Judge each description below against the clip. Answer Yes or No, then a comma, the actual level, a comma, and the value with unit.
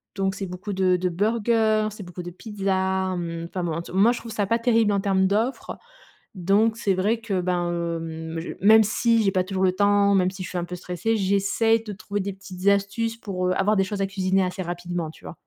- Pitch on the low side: No, high, 195 Hz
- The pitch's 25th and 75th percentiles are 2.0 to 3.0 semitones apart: Yes, narrow, 2.6 semitones